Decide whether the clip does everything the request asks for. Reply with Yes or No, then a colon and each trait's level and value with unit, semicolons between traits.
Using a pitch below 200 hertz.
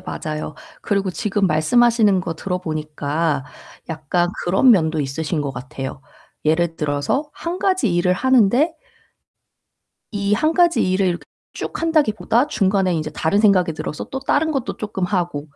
Yes: medium, 185 Hz